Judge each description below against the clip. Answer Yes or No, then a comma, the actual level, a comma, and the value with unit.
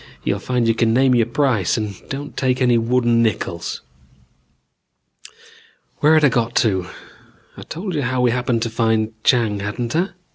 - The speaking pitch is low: Yes, low, 120 Hz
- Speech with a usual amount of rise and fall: No, narrow, 2.3 semitones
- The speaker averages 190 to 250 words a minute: No, average, 170 wpm